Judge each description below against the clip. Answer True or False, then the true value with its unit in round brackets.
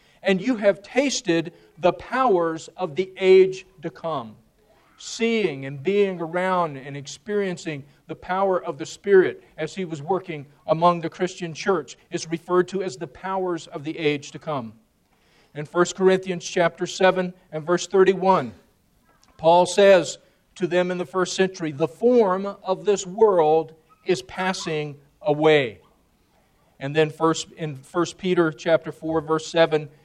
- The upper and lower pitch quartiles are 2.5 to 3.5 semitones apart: True (3.0 semitones)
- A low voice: False (175 Hz)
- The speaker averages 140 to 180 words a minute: True (150 wpm)